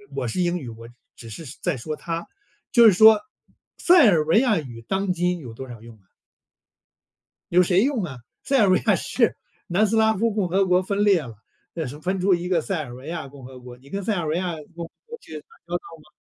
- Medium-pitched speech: Yes, medium, 175 Hz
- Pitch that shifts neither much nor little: No, wide, 6.1 semitones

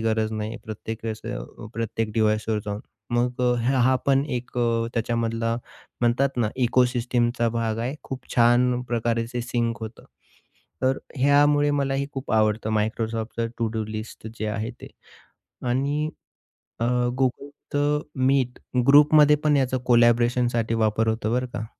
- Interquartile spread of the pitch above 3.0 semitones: No, narrow, 2.5 semitones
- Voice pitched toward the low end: Yes, low, 120 Hz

